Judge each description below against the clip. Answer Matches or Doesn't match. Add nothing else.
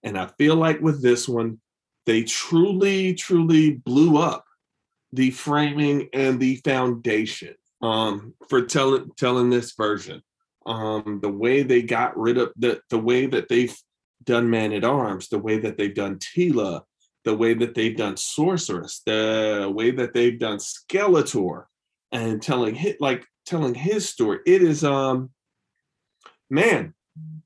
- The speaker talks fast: Doesn't match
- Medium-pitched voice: Doesn't match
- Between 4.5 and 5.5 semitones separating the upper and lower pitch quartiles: Matches